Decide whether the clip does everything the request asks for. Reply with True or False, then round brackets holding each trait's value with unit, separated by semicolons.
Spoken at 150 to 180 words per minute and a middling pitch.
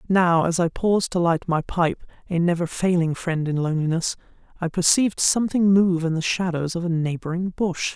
True (175 wpm; 175 Hz)